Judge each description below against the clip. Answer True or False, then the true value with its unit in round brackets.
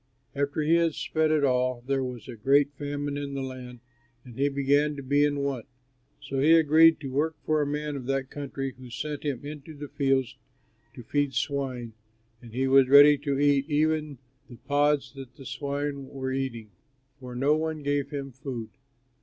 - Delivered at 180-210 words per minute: True (190 wpm)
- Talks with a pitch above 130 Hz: True (140 Hz)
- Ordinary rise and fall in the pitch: False (1.8 semitones)